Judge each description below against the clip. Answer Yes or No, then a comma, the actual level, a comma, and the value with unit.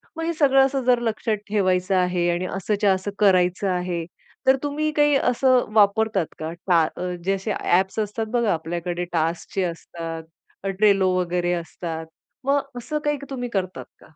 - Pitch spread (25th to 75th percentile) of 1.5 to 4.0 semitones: No, wide, 5.4 semitones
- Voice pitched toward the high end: Yes, high, 195 Hz